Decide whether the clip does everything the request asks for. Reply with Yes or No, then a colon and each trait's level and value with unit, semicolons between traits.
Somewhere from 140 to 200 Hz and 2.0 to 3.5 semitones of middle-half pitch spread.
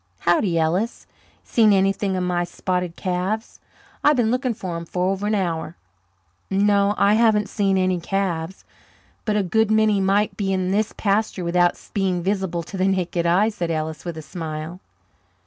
Yes: high, 190 Hz; average, 2.9 semitones